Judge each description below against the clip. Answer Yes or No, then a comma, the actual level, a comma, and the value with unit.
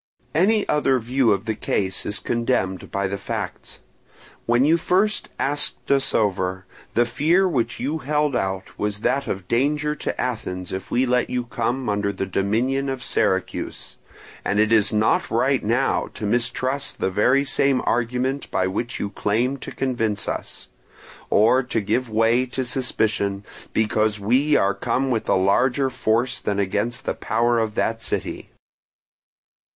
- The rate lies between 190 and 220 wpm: No, average, 155 wpm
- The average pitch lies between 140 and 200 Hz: No, low, 120 Hz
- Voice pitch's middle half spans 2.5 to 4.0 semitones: No, average, 4.5 semitones